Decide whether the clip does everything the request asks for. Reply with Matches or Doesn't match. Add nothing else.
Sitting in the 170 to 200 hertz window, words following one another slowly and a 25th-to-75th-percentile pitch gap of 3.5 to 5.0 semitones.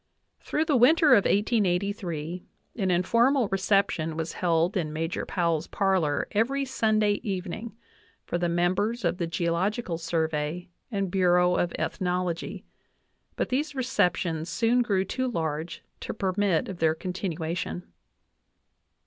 Matches